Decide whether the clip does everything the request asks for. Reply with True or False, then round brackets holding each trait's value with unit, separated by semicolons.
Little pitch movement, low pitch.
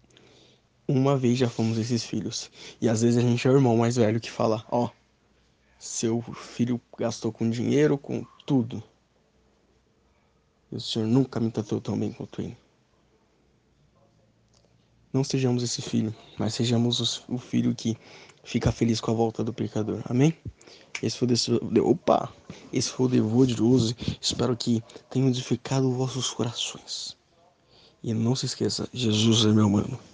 True (2.1 semitones; 115 Hz)